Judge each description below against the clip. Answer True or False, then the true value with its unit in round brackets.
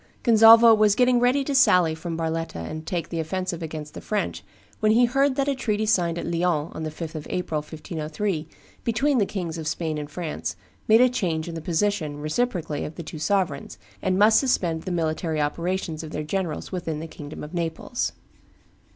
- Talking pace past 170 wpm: True (195 wpm)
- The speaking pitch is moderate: True (170 Hz)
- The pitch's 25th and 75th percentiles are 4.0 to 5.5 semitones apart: True (5.2 semitones)